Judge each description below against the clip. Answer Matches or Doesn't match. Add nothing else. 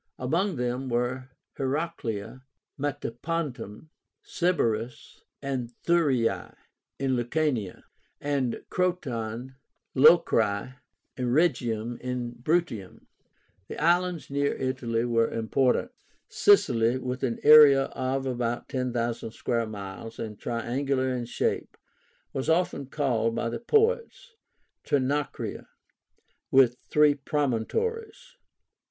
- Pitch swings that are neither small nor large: Matches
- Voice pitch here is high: Doesn't match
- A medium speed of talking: Doesn't match